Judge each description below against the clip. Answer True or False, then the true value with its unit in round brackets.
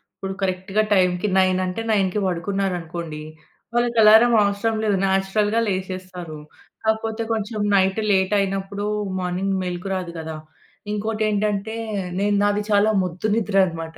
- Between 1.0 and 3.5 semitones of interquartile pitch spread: True (2.4 semitones)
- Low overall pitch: False (195 Hz)